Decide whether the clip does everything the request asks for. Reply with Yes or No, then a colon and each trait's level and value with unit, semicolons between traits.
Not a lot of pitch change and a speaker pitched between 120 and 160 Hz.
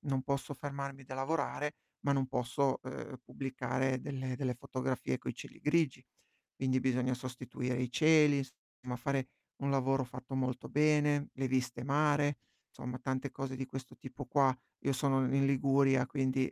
Yes: narrow, 1.5 semitones; low, 135 Hz